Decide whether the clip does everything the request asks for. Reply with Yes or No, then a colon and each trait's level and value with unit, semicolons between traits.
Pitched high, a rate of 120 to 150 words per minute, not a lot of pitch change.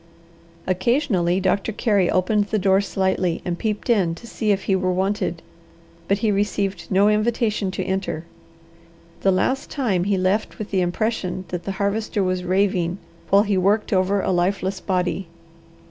No: high, 195 Hz; average, 160 wpm; narrow, 2.1 semitones